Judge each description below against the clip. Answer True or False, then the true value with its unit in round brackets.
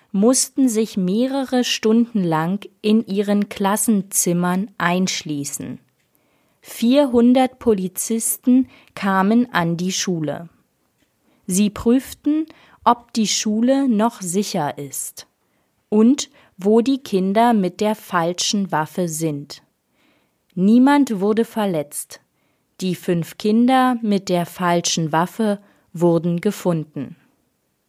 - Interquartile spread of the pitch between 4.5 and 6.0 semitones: True (4.8 semitones)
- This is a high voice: True (205 Hz)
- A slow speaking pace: True (95 wpm)